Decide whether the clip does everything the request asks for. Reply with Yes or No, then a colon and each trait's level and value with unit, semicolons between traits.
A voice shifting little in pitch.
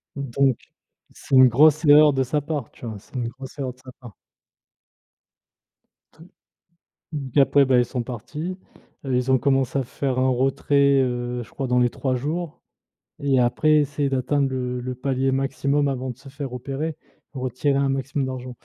Yes: narrow, 1.9 semitones